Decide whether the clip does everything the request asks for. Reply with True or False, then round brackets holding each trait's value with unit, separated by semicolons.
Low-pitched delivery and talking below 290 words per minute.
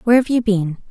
False (215 Hz; 265 wpm)